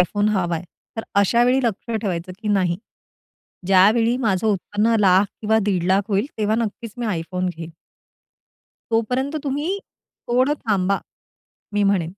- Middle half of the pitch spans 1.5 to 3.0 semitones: No, average, 3.8 semitones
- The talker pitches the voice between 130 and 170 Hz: No, high, 205 Hz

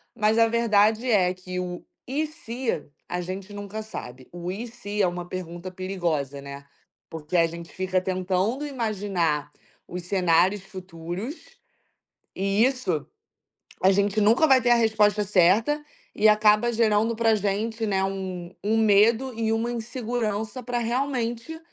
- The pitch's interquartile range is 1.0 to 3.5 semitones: No, average, 4.0 semitones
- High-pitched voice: Yes, high, 205 Hz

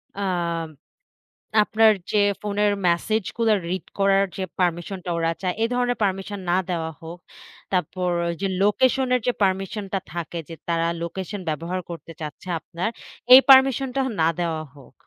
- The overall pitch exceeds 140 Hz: Yes, high, 190 Hz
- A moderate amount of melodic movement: Yes, average, 3.7 semitones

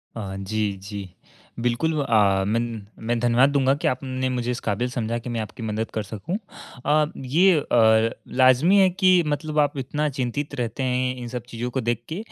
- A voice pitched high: No, low, 125 Hz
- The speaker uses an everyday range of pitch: Yes, average, 3.9 semitones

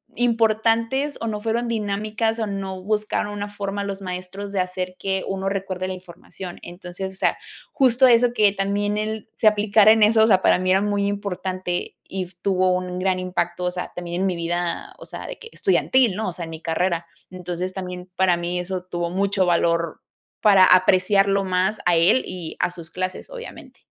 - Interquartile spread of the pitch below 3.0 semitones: Yes, narrow, 2.6 semitones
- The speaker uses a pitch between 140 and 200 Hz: Yes, high, 190 Hz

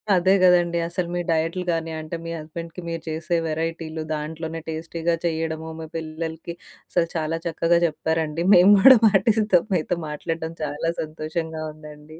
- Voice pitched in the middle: Yes, medium, 165 Hz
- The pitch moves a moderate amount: No, narrow, 1.3 semitones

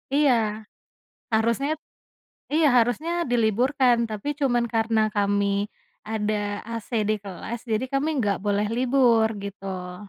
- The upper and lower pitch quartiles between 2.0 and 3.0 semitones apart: No, average, 3.8 semitones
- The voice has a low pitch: No, high, 225 Hz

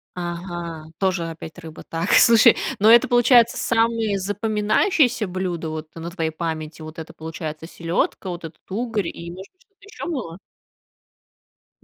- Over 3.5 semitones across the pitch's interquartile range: Yes, wide, 5.4 semitones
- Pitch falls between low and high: Yes, medium, 180 Hz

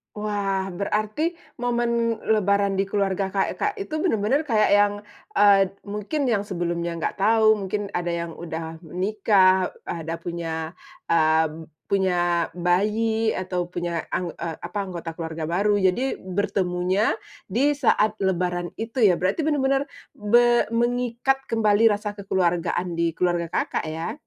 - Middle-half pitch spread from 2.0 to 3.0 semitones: No, average, 4.0 semitones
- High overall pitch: Yes, high, 195 Hz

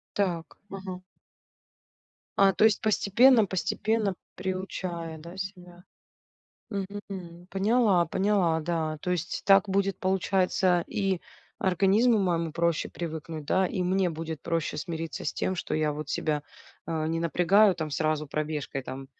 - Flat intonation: No, average, 3.1 semitones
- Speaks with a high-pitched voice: No, medium, 180 Hz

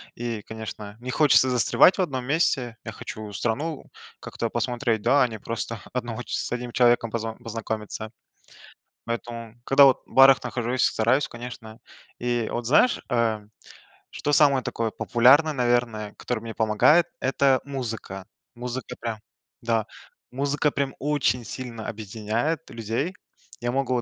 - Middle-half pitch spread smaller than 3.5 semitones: Yes, average, 3.0 semitones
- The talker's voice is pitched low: Yes, low, 120 Hz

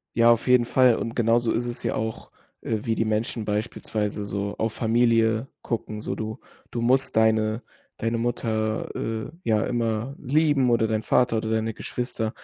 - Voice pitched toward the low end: Yes, low, 115 Hz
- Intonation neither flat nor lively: No, narrow, 1.6 semitones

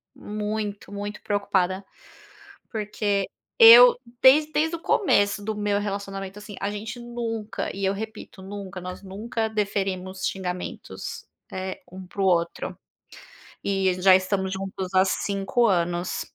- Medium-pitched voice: No, high, 200 Hz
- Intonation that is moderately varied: No, narrow, 2.0 semitones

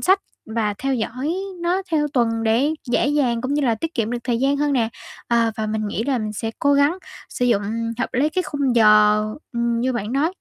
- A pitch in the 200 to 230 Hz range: No, high, 245 Hz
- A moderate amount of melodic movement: Yes, average, 4.2 semitones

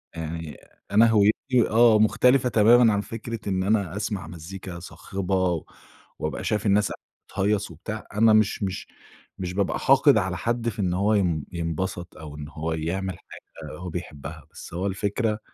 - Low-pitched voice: Yes, low, 100 Hz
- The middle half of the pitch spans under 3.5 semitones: No, average, 3.8 semitones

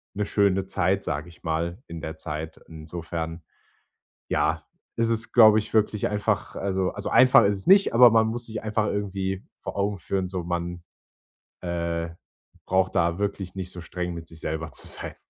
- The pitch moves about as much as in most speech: Yes, average, 3.4 semitones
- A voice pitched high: No, very low, 95 Hz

